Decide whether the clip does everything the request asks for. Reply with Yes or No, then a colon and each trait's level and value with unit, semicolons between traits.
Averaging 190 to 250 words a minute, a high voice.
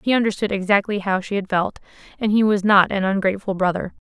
Yes: fast, 205 wpm; high, 200 Hz